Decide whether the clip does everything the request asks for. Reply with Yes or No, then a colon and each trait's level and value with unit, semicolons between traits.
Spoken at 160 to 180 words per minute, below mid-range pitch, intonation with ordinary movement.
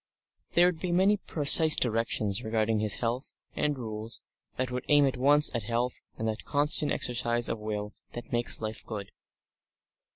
Yes: average, 165 wpm; low, 120 Hz; average, 4.8 semitones